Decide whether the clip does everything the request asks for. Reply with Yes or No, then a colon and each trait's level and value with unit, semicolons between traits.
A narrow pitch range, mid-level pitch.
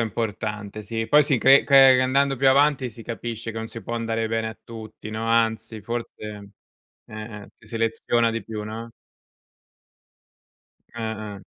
No: narrow, 1.5 semitones; low, 115 Hz